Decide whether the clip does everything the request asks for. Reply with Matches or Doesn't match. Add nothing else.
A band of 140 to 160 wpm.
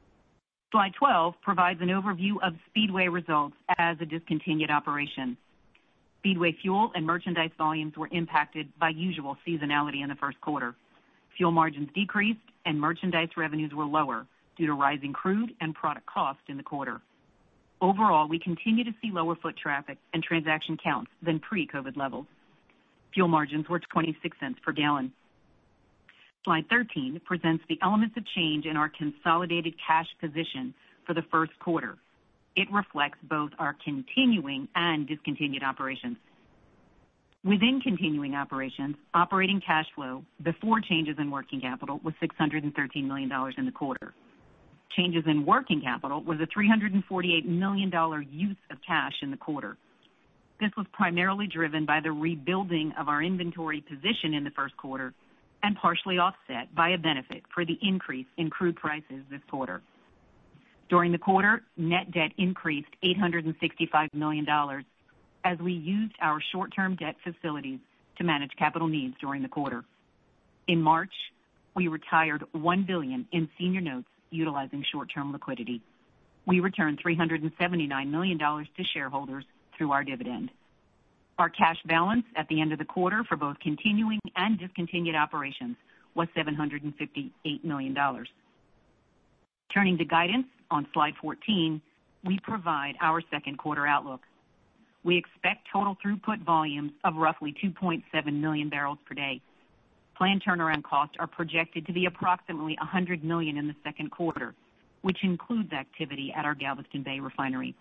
Matches